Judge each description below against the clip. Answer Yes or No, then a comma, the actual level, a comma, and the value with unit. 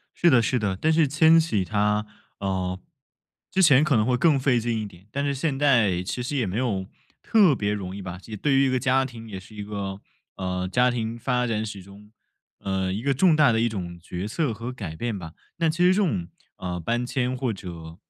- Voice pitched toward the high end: No, low, 115 Hz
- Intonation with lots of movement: Yes, wide, 5.7 semitones